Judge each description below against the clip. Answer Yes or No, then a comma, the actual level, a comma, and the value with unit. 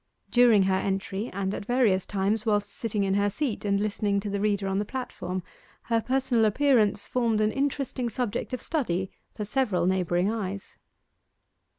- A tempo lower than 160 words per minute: No, average, 170 wpm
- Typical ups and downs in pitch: Yes, average, 3.5 semitones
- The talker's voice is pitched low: No, high, 210 Hz